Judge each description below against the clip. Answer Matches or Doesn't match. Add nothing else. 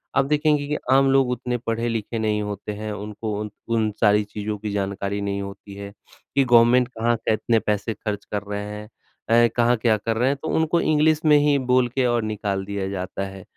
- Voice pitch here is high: Doesn't match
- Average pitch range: Matches